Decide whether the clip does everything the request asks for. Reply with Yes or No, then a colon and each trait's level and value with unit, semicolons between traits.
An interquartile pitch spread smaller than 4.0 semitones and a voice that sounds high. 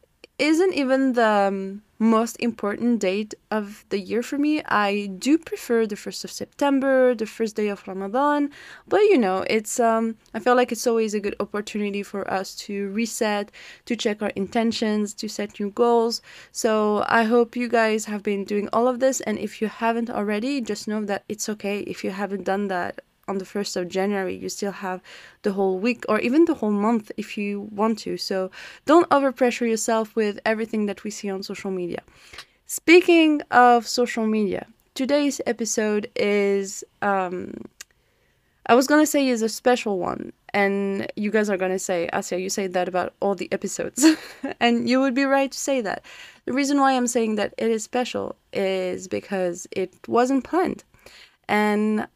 Yes: average, 3.4 semitones; high, 215 Hz